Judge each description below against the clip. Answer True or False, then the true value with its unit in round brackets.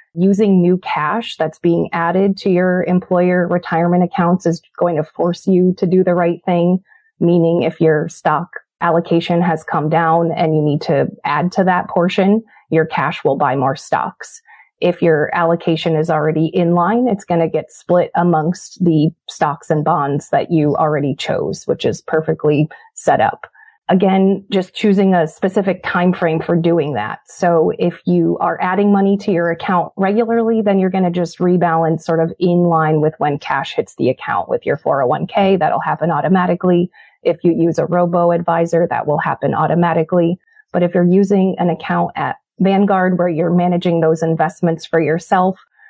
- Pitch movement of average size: False (2.2 semitones)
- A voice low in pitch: False (175 Hz)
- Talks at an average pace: True (180 wpm)